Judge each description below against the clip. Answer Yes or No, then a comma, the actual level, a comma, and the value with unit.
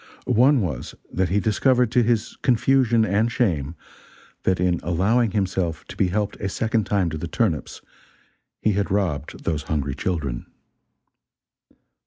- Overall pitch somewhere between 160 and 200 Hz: No, low, 100 Hz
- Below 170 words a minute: Yes, average, 145 wpm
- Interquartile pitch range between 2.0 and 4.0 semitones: No, average, 5.2 semitones